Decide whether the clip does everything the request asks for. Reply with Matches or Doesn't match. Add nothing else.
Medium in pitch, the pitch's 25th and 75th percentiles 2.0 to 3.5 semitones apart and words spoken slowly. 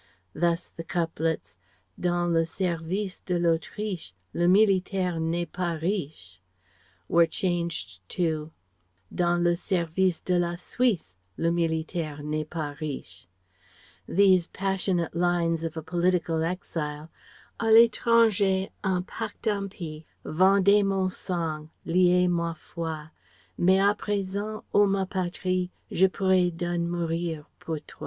Matches